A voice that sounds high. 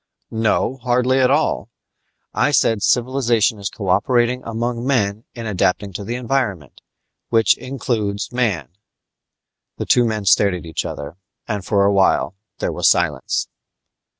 No: low, 115 Hz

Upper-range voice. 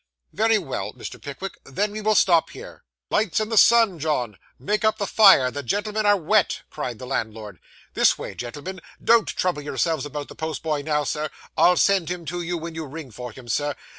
No: medium, 165 Hz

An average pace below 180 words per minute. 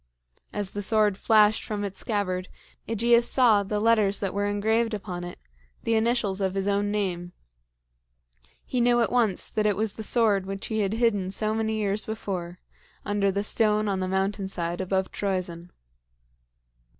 Yes: average, 170 wpm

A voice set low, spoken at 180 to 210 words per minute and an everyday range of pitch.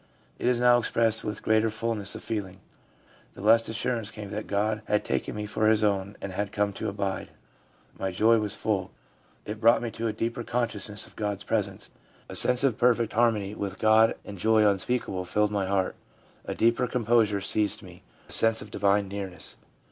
No: low, 105 Hz; average, 200 wpm; narrow, 2.0 semitones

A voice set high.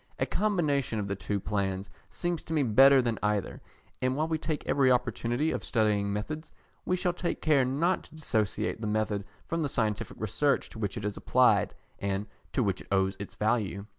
No: low, 115 Hz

